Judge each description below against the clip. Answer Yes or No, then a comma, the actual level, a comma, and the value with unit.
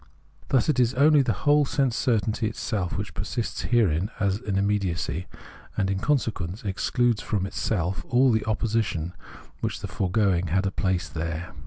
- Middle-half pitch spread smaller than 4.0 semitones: No, average, 4.4 semitones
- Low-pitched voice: Yes, low, 105 Hz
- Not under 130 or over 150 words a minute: No, average, 165 wpm